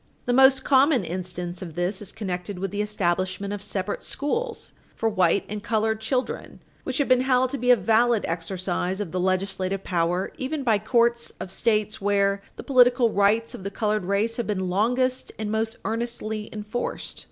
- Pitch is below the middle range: No, high, 210 Hz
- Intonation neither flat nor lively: Yes, average, 4.1 semitones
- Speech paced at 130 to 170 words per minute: No, average, 180 wpm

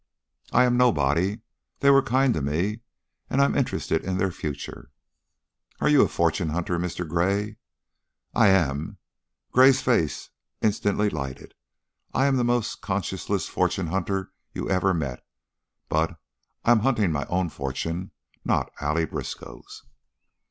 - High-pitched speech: No, very low, 95 Hz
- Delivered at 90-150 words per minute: Yes, average, 140 wpm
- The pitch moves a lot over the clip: Yes, wide, 6.5 semitones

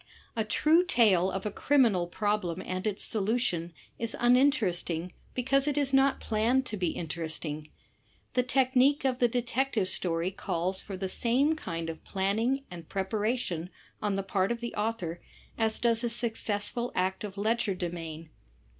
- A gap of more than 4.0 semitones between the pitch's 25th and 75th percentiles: Yes, average, 5.3 semitones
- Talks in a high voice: Yes, high, 210 Hz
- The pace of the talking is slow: No, average, 155 wpm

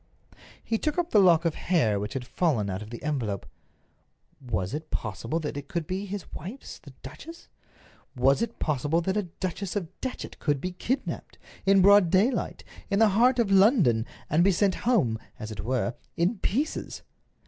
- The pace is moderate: Yes, average, 180 wpm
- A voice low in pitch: No, medium, 170 Hz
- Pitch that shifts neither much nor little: No, wide, 7.8 semitones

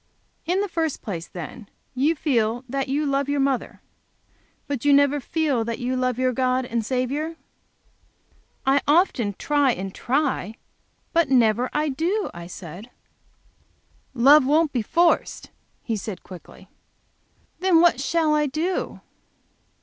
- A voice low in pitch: No, very high, 270 Hz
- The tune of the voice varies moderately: Yes, average, 4.3 semitones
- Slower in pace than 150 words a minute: Yes, average, 140 wpm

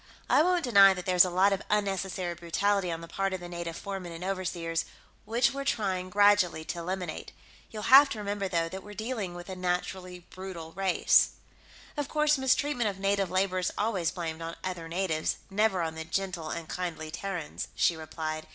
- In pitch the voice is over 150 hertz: Yes, medium, 185 Hz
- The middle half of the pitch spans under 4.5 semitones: Yes, average, 2.9 semitones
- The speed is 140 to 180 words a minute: No, average, 190 wpm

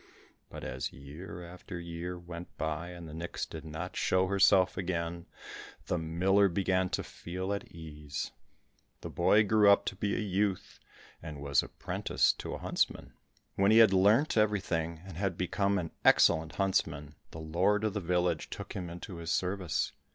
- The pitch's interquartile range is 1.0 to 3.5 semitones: Yes, average, 2.9 semitones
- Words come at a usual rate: Yes, average, 170 wpm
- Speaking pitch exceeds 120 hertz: No, very low, 90 Hz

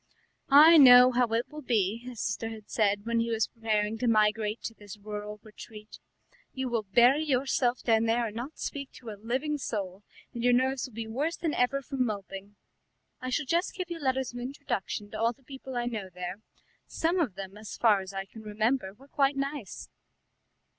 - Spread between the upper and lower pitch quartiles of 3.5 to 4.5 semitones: Yes, average, 3.9 semitones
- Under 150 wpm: No, average, 200 wpm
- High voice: Yes, high, 235 Hz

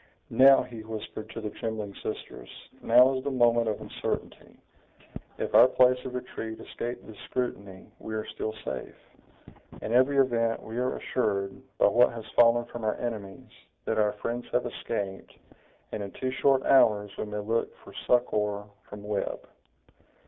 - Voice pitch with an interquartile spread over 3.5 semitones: No, average, 2.9 semitones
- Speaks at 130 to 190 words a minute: Yes, average, 165 wpm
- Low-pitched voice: Yes, low, 115 Hz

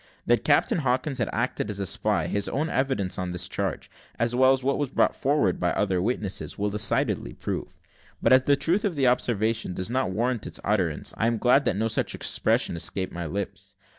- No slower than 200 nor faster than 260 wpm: Yes, fast, 205 wpm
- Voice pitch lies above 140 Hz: No, low, 115 Hz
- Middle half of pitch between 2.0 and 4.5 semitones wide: No, average, 4.9 semitones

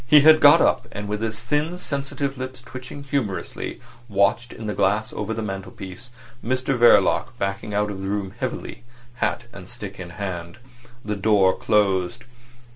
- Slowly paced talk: No, average, 165 wpm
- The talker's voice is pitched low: Yes, low, 105 Hz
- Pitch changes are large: No, average, 4.7 semitones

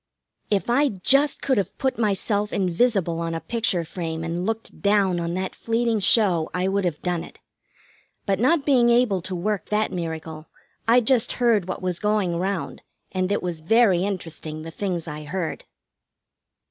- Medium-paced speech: Yes, average, 170 wpm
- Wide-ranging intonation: No, average, 4.7 semitones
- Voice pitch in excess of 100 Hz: Yes, high, 190 Hz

